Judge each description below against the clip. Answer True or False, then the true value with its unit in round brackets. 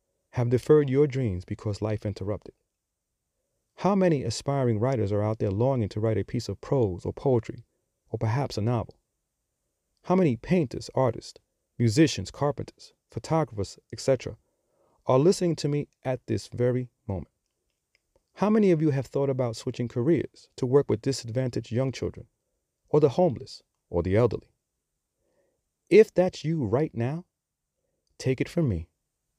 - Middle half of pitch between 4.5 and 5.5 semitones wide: True (5.1 semitones)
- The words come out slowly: False (150 wpm)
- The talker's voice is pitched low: True (125 Hz)